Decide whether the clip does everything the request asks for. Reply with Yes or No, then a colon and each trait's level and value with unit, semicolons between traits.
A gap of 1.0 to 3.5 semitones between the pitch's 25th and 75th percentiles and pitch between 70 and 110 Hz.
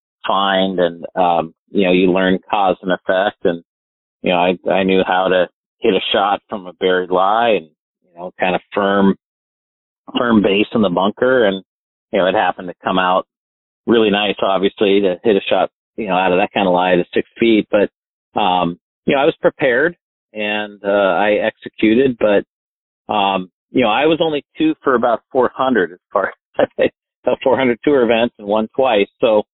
Yes: average, 2.9 semitones; very low, 95 Hz